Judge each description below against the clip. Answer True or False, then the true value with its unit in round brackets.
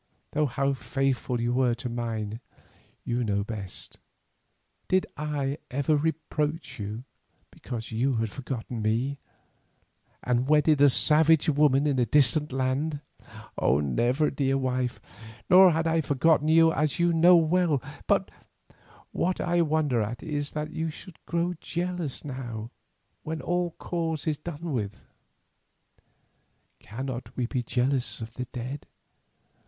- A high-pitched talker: False (140 Hz)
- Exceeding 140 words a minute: False (135 wpm)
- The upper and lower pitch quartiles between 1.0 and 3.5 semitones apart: False (4.5 semitones)